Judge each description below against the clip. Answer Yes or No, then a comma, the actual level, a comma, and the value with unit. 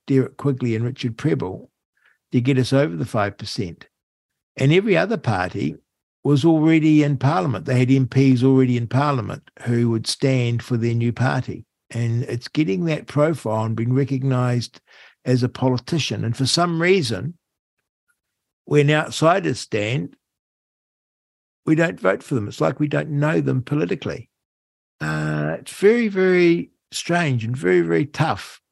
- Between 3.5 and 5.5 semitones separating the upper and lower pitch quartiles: Yes, average, 4.3 semitones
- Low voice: Yes, low, 130 Hz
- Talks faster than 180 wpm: No, average, 150 wpm